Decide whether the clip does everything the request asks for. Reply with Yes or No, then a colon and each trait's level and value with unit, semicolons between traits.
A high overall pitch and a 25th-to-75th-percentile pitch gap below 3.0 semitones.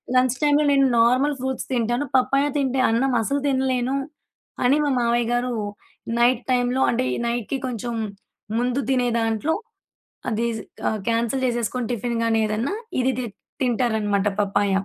Yes: high, 245 Hz; narrow, 2.4 semitones